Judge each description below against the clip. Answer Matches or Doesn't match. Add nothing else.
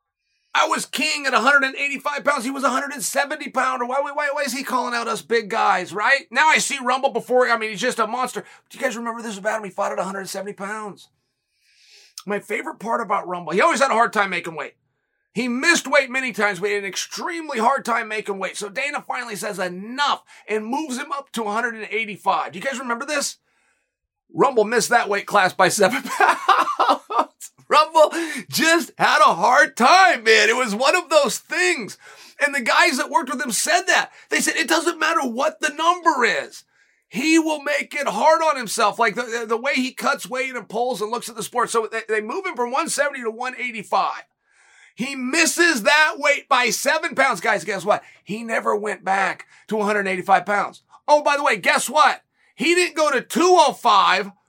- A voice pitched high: Matches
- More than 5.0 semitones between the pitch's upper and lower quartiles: Matches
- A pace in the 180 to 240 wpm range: Matches